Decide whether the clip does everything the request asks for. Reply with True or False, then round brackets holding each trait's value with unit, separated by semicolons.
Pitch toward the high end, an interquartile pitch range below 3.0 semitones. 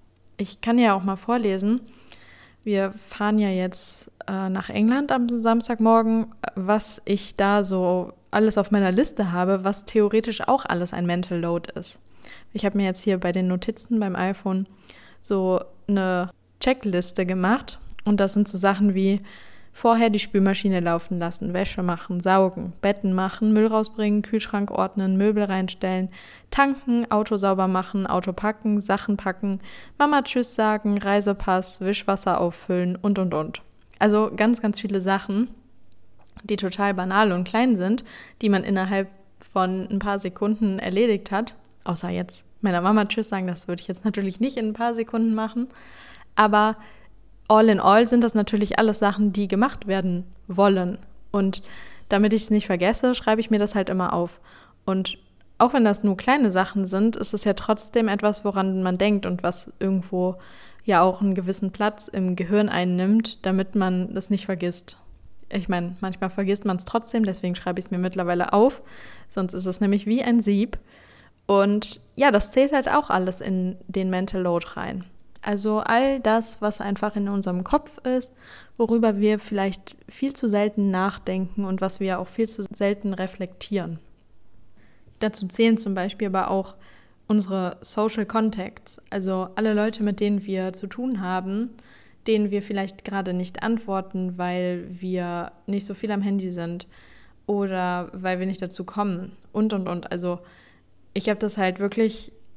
True (200 Hz; 2.4 semitones)